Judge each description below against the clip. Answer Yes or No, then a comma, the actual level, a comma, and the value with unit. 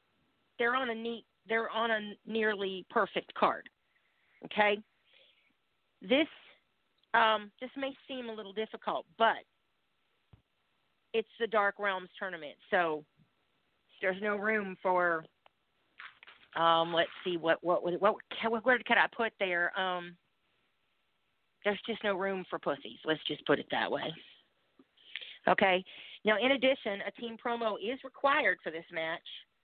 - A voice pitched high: Yes, high, 210 Hz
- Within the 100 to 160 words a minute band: Yes, slow, 135 wpm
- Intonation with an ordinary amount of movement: Yes, average, 3.9 semitones